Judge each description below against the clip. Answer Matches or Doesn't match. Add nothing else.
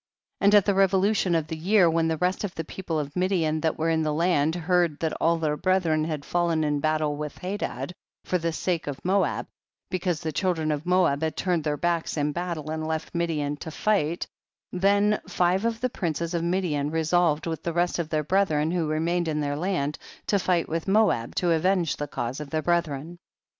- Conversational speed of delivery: Doesn't match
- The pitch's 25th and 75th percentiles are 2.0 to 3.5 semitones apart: Matches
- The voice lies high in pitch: Doesn't match